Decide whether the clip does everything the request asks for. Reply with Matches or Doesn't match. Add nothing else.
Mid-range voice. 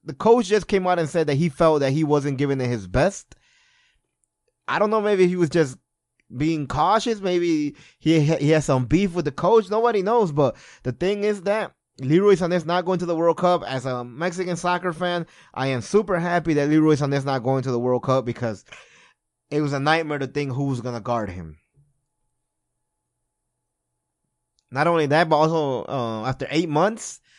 Matches